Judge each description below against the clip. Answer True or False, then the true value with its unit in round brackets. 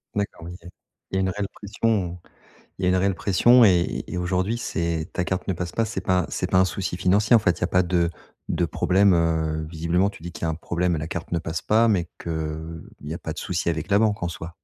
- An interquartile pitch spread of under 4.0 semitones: True (2.5 semitones)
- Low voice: True (90 Hz)